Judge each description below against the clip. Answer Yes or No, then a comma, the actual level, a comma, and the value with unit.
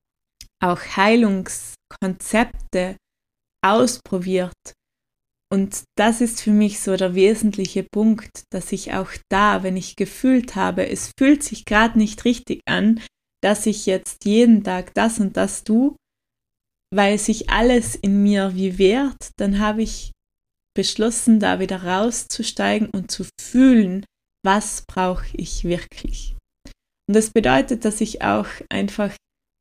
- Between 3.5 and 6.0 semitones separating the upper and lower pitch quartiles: No, average, 2.8 semitones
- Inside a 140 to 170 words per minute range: No, average, 130 wpm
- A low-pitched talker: No, high, 205 Hz